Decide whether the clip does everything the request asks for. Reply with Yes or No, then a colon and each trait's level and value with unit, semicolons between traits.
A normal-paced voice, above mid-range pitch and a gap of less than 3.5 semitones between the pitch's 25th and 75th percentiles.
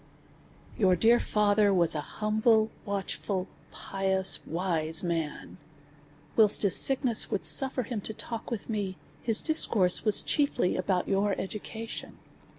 No: slow, 130 wpm; high, 205 Hz; average, 3.1 semitones